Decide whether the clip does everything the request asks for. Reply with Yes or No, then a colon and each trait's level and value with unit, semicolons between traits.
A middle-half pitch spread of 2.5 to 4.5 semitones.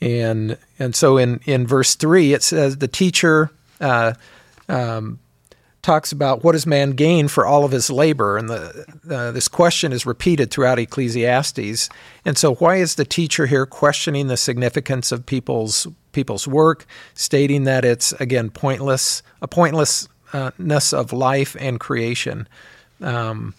Yes: average, 3.6 semitones